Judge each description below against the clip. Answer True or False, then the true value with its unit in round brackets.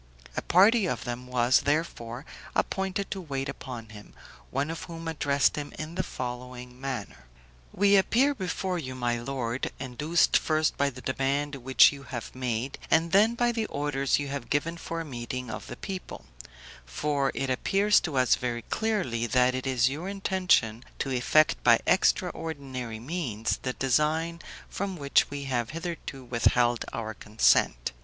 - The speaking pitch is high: False (135 Hz)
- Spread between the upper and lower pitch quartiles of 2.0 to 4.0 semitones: False (5.0 semitones)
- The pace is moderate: True (165 wpm)